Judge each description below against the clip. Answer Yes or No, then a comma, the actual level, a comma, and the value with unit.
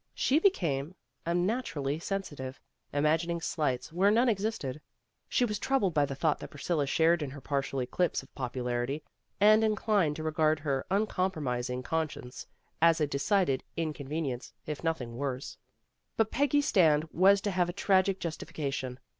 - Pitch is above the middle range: No, medium, 160 Hz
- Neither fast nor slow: Yes, average, 155 wpm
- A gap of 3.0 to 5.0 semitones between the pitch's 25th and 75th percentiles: No, wide, 5.6 semitones